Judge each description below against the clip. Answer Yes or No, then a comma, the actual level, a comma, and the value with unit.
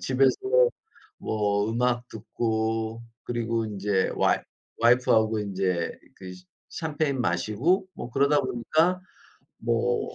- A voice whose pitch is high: No, low, 115 Hz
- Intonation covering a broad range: No, average, 4.3 semitones